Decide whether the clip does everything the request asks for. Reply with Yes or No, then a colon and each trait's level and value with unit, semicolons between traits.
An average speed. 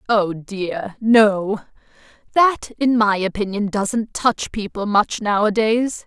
No: slow, 120 wpm